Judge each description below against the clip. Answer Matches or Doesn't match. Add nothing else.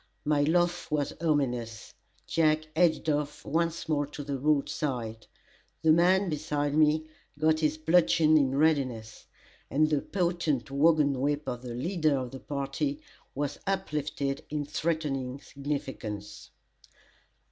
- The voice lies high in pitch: Doesn't match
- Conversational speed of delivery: Doesn't match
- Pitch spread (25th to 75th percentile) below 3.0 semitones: Matches